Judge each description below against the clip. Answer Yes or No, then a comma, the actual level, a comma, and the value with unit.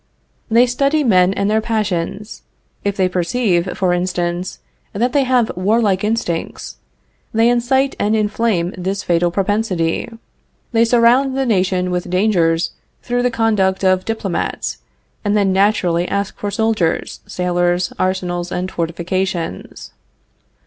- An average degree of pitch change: Yes, average, 4.0 semitones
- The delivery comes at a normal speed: No, slow, 130 wpm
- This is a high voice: Yes, high, 195 Hz